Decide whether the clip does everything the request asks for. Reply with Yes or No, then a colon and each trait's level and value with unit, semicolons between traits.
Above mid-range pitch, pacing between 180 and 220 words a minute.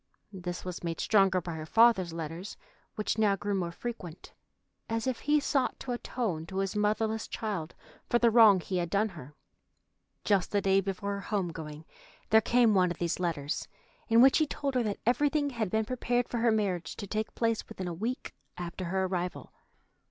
Yes: high, 200 Hz; average, 195 wpm